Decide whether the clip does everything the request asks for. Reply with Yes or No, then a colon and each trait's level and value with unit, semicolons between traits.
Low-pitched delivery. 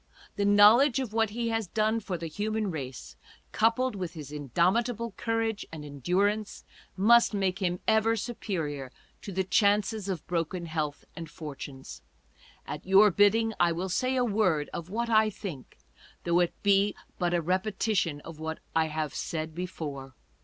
No: high, 190 Hz